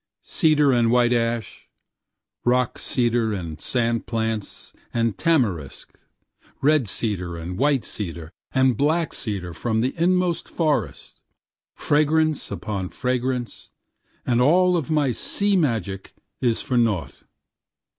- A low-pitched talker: Yes, low, 120 Hz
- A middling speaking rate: No, slow, 115 wpm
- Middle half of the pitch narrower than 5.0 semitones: No, wide, 5.6 semitones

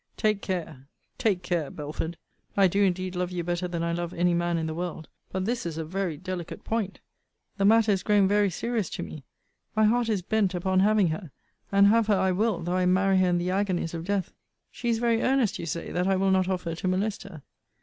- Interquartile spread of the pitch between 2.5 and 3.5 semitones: Yes, average, 2.8 semitones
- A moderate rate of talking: No, fast, 230 wpm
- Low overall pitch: No, medium, 185 Hz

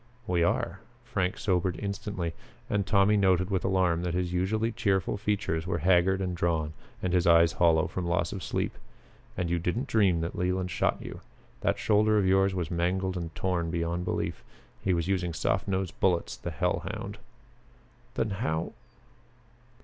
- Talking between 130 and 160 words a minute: No, average, 170 wpm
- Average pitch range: No, narrow, 2.1 semitones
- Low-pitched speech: Yes, very low, 90 Hz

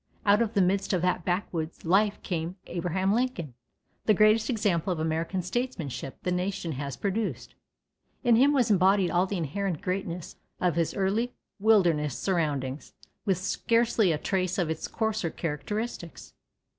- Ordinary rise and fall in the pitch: Yes, average, 4.0 semitones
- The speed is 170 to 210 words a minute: No, average, 150 wpm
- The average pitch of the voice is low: No, medium, 185 Hz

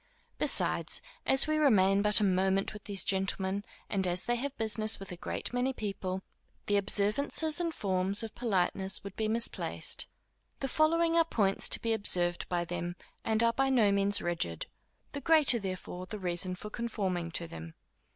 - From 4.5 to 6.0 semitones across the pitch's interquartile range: No, average, 4.1 semitones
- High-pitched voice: Yes, high, 200 Hz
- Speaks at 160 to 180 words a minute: Yes, average, 175 wpm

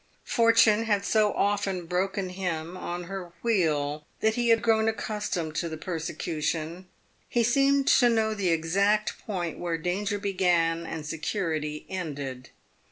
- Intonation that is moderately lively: Yes, average, 4.5 semitones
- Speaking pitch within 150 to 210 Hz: Yes, medium, 185 Hz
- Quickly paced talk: No, average, 140 wpm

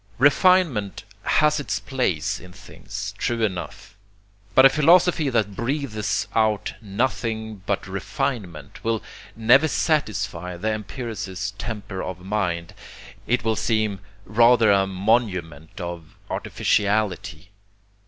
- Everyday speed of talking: No, slow, 110 wpm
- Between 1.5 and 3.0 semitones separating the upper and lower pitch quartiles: No, average, 4.0 semitones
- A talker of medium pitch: No, low, 110 Hz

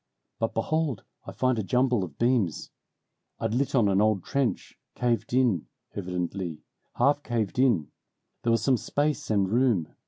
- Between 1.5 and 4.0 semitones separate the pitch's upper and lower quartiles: No, average, 4.8 semitones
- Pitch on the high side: No, low, 115 Hz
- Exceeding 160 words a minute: No, average, 155 wpm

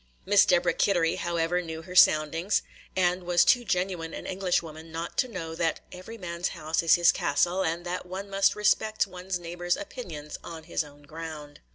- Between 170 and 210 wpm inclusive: Yes, average, 180 wpm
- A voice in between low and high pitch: Yes, medium, 175 Hz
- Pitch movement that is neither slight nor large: No, narrow, 2.3 semitones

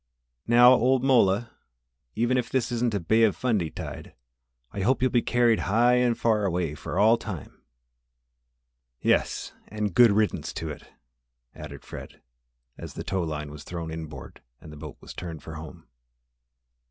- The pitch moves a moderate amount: No, wide, 6.5 semitones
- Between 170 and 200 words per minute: No, average, 160 wpm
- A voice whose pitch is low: Yes, low, 105 Hz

